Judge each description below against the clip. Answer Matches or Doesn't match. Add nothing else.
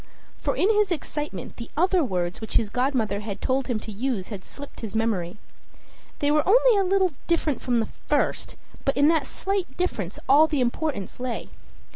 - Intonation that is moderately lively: Doesn't match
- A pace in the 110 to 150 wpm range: Doesn't match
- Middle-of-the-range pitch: Doesn't match